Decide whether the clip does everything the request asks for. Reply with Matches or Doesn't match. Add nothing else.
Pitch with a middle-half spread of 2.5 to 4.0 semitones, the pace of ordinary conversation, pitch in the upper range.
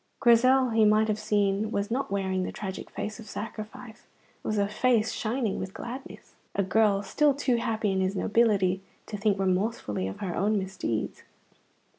Matches